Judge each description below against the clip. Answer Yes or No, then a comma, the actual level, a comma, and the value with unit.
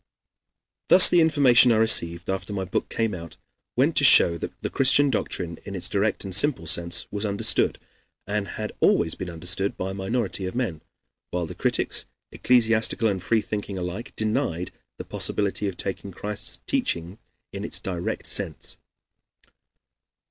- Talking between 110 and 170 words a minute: Yes, average, 155 wpm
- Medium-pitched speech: No, low, 100 Hz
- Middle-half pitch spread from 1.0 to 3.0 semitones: No, average, 3.7 semitones